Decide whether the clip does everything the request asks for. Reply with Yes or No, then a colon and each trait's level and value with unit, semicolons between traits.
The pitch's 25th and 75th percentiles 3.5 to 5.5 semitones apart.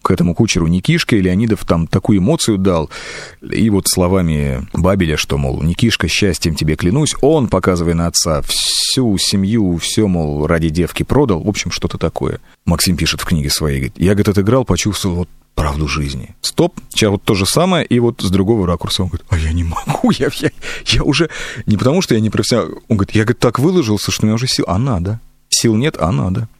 Yes: average, 5.0 semitones